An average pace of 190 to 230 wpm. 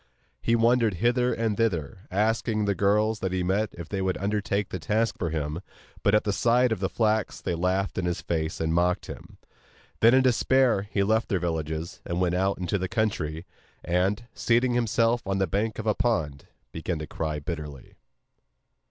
Yes: average, 195 wpm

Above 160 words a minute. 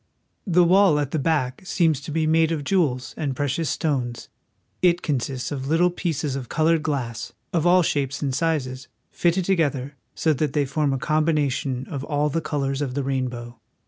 Yes: average, 185 wpm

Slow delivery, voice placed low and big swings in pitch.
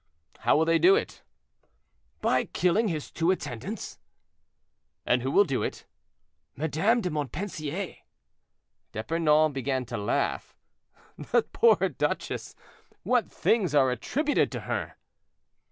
No: slow, 120 wpm; medium, 160 Hz; wide, 6.7 semitones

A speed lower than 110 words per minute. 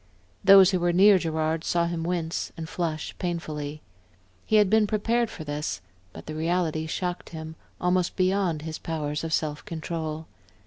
No: average, 165 wpm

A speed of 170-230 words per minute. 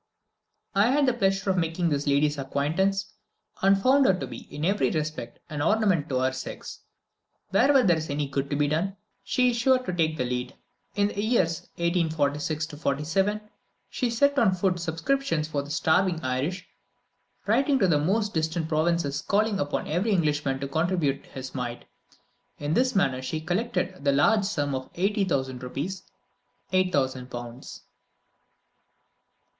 No: average, 160 wpm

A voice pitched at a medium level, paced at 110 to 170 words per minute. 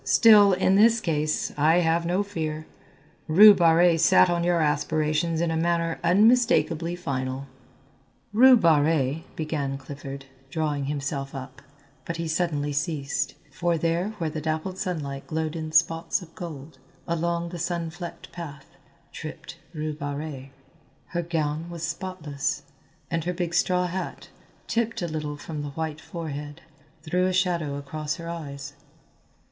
Yes: medium, 160 Hz; average, 145 wpm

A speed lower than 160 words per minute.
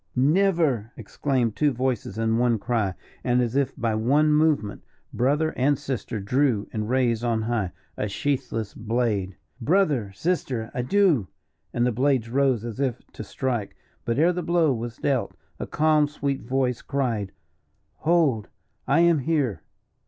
Yes: average, 150 wpm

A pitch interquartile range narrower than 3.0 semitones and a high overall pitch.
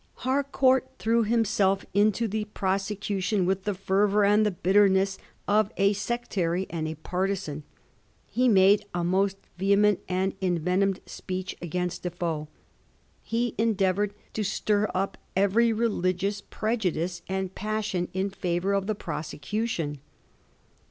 Yes: narrow, 2.5 semitones; high, 195 Hz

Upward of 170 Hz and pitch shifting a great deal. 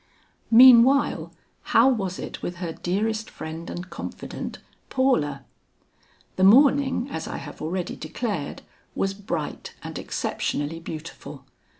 Yes: high, 190 Hz; wide, 6.7 semitones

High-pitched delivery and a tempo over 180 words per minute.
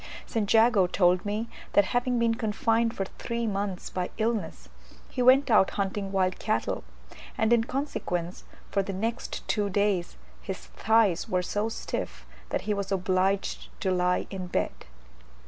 No: high, 205 Hz; average, 155 wpm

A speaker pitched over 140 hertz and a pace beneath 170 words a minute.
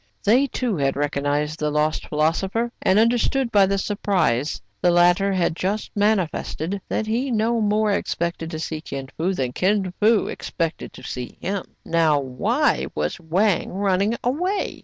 Yes: medium, 185 Hz; average, 160 wpm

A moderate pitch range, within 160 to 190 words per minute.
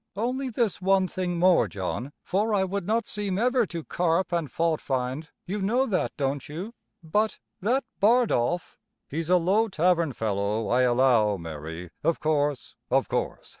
No: wide, 7.4 semitones; average, 165 wpm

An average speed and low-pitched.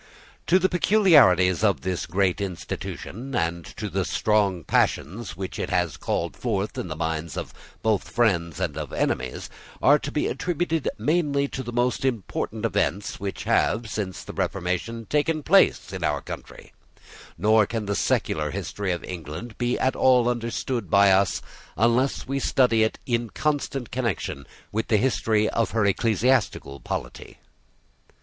Yes: average, 155 wpm; low, 110 Hz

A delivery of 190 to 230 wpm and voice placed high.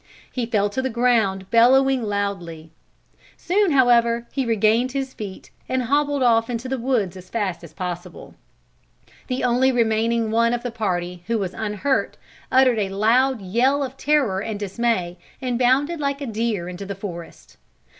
No: average, 165 wpm; high, 230 Hz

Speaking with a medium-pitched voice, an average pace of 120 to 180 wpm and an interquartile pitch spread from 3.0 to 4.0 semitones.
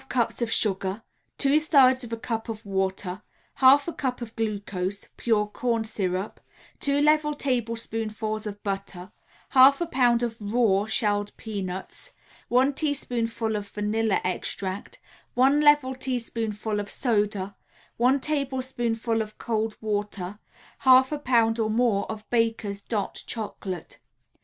No: high, 225 Hz; slow, 135 wpm; average, 3.6 semitones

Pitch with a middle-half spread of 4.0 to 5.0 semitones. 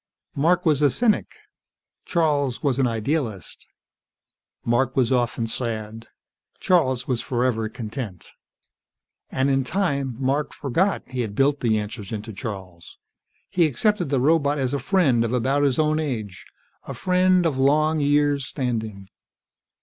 Yes: average, 4.4 semitones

